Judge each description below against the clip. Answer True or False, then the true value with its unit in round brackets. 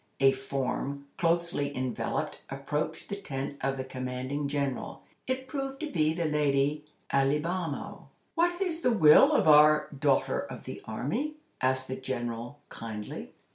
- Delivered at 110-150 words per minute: True (140 wpm)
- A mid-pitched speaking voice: True (145 Hz)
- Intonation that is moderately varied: True (4.2 semitones)